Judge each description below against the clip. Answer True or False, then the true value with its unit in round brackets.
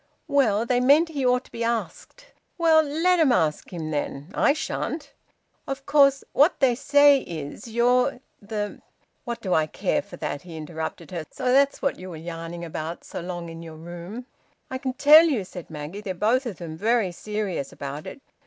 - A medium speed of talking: True (195 wpm)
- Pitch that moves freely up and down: True (8.3 semitones)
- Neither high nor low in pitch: False (215 Hz)